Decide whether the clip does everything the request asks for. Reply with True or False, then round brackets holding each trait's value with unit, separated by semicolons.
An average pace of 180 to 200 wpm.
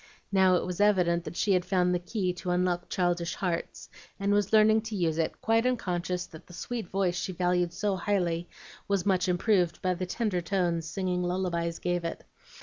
True (195 wpm)